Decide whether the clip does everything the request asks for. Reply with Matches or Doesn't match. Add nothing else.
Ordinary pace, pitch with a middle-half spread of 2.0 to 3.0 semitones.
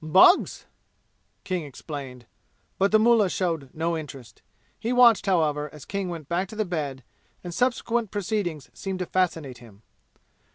Doesn't match